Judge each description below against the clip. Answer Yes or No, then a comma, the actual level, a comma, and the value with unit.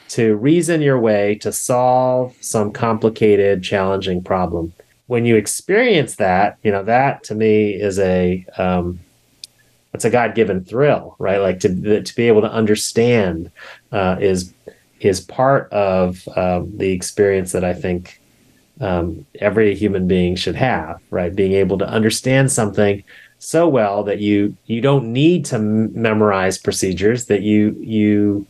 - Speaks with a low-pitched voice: Yes, low, 105 Hz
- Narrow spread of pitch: No, average, 3.2 semitones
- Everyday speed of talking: Yes, average, 150 wpm